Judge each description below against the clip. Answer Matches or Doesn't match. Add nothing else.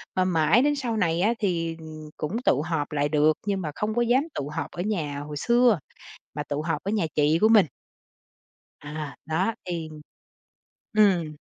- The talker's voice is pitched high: Doesn't match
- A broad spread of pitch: Matches